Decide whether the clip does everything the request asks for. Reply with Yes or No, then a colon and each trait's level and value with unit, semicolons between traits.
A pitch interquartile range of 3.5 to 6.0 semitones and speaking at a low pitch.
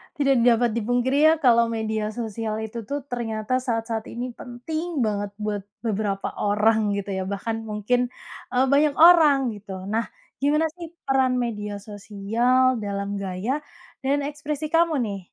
No: average, 4.0 semitones; high, 230 Hz